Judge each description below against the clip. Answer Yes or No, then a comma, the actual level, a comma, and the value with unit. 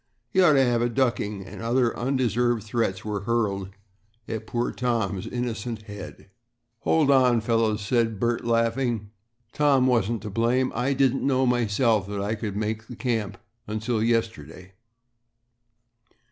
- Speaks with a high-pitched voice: No, low, 115 Hz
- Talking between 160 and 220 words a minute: No, average, 145 wpm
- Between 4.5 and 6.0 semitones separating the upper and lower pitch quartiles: No, average, 2.7 semitones